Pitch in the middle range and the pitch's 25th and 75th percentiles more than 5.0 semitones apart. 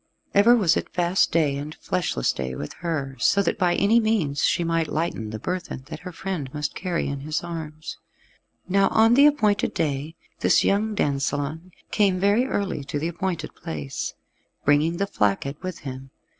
Yes: medium, 165 Hz; wide, 5.4 semitones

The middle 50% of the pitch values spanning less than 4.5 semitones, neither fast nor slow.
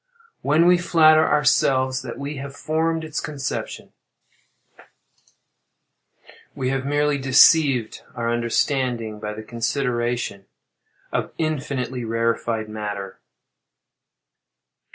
No: average, 4.1 semitones; slow, 90 wpm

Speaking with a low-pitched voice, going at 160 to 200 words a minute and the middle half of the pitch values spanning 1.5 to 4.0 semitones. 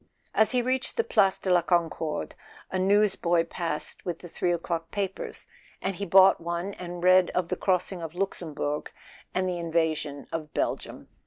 No: medium, 175 Hz; average, 170 wpm; narrow, 2.5 semitones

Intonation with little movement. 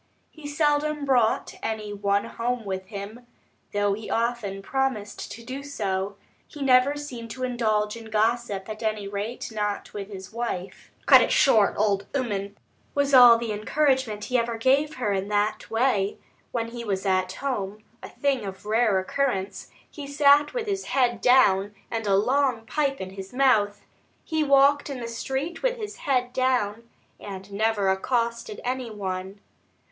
No: average, 4.6 semitones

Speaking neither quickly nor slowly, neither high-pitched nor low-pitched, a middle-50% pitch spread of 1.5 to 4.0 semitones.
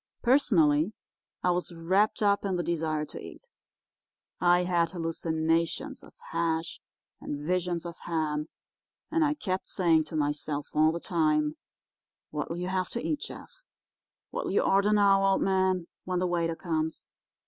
Yes: average, 150 wpm; medium, 170 Hz; average, 2.9 semitones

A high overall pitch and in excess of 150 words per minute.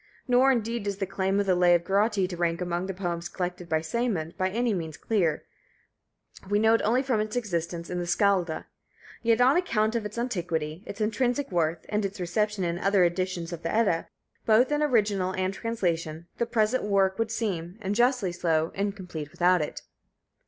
Yes: high, 195 Hz; average, 195 wpm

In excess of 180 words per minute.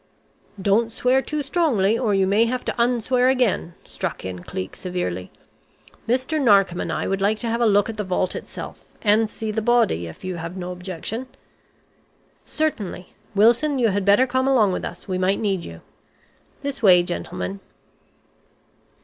No: average, 175 wpm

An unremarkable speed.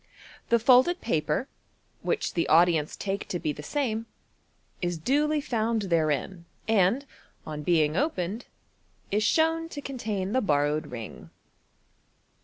No: slow, 125 wpm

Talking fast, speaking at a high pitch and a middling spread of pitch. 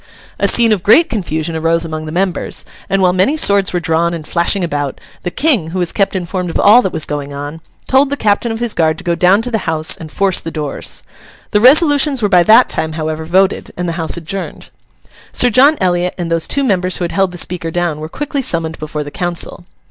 No: fast, 230 wpm; medium, 180 Hz; average, 4.3 semitones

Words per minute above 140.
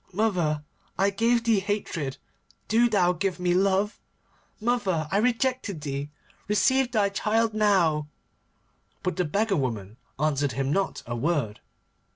No: slow, 135 wpm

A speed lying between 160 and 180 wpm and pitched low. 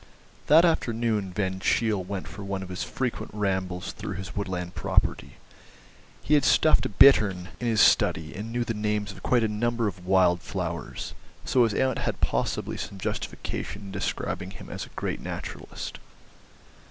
Yes: average, 170 wpm; low, 100 Hz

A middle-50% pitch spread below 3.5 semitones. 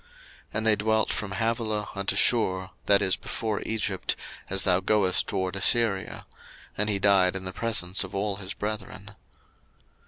Yes: narrow, 2.4 semitones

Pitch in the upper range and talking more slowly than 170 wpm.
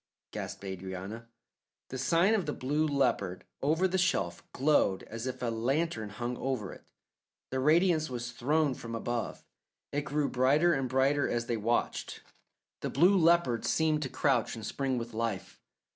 No: low, 130 Hz; average, 160 wpm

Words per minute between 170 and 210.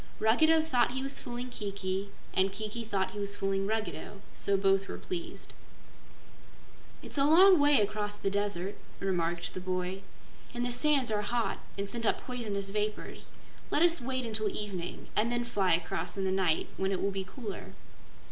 Yes: average, 175 wpm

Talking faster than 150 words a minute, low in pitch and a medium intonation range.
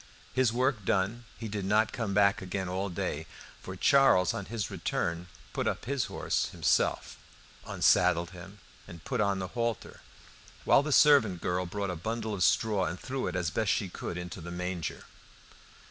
Yes: average, 175 wpm; low, 100 Hz; average, 4.0 semitones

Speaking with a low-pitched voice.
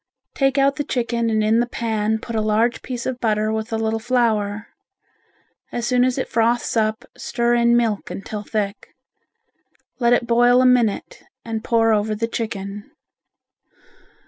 No: high, 230 Hz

